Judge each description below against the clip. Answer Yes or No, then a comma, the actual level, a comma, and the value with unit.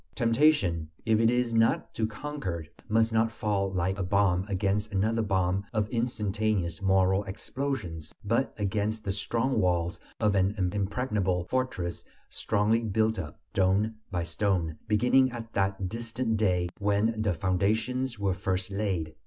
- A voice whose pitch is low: Yes, low, 105 Hz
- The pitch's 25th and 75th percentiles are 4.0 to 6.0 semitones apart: No, average, 3.2 semitones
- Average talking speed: Yes, average, 145 wpm